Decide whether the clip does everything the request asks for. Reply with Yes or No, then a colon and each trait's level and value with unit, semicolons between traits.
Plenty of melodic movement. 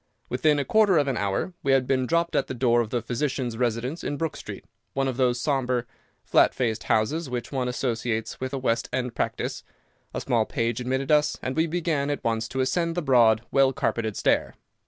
No: average, 3.4 semitones